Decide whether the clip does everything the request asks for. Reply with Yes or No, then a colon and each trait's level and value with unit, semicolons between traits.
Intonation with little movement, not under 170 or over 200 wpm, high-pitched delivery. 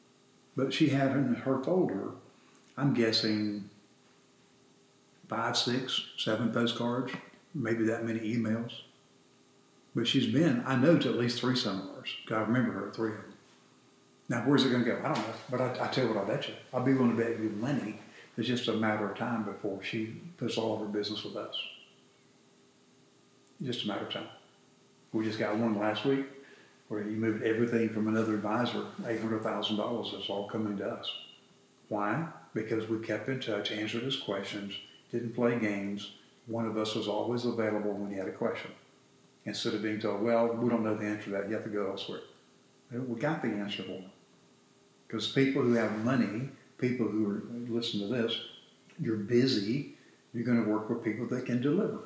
No: narrow, 2.2 semitones; average, 190 wpm; low, 110 Hz